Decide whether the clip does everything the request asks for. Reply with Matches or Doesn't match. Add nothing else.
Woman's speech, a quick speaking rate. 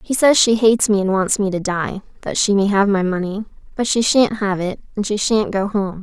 Matches